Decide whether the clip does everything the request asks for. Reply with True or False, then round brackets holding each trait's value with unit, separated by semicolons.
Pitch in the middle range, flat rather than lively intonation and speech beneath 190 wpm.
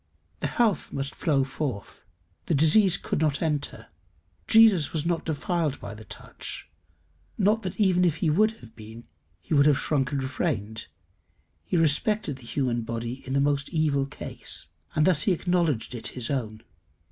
False (145 Hz; 4.8 semitones; 165 wpm)